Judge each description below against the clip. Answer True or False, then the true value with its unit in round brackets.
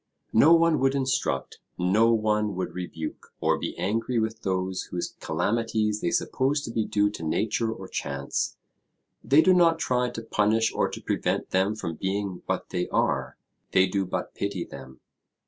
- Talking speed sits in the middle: True (170 wpm)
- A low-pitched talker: True (105 Hz)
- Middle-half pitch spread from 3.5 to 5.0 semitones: True (4.0 semitones)